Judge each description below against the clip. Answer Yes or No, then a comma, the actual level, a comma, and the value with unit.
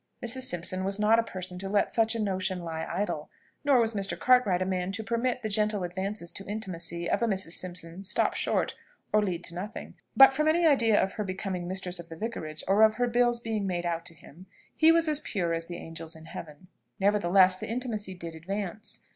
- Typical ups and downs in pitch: Yes, average, 4.1 semitones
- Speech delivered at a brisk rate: Yes, fast, 220 wpm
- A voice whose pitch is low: No, high, 195 Hz